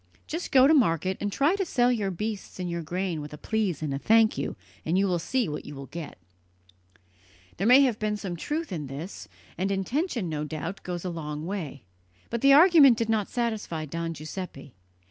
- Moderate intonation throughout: No, wide, 6.3 semitones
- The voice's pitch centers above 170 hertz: Yes, high, 190 Hz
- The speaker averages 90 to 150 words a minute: No, fast, 205 wpm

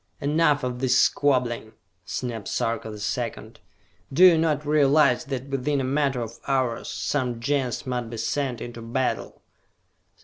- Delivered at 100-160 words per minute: Yes, average, 145 wpm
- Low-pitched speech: Yes, low, 130 Hz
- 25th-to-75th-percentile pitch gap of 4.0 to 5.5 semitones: No, average, 3.3 semitones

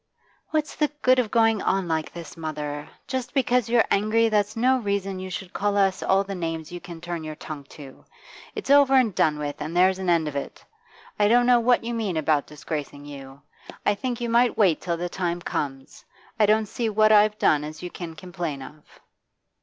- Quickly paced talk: Yes, fast, 210 wpm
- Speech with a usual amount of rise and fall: No, wide, 6.1 semitones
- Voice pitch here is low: No, high, 190 Hz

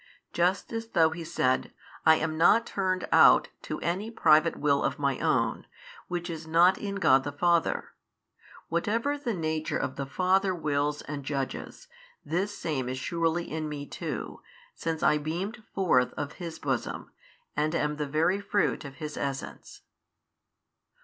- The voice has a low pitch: No, medium, 160 Hz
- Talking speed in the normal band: Yes, average, 155 wpm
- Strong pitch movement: No, average, 3.9 semitones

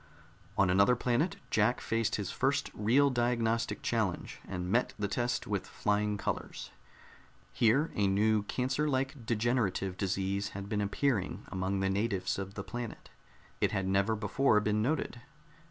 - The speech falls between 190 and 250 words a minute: No, average, 150 wpm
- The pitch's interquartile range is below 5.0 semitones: Yes, average, 3.6 semitones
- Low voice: Yes, low, 110 Hz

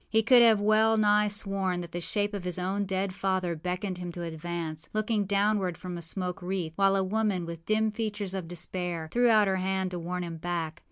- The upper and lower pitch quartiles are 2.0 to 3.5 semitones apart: Yes, average, 2.9 semitones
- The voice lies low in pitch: No, high, 190 Hz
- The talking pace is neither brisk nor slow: No, fast, 220 wpm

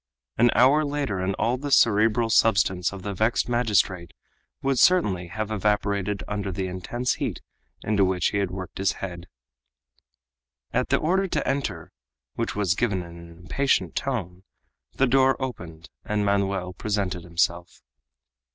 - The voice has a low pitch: Yes, low, 100 Hz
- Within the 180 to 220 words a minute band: No, average, 150 wpm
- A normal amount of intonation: Yes, average, 4.7 semitones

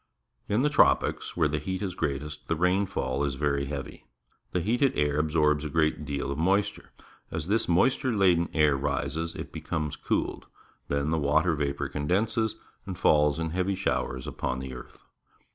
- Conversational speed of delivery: Yes, average, 170 wpm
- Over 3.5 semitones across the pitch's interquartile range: Yes, average, 4.2 semitones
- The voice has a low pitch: Yes, very low, 75 Hz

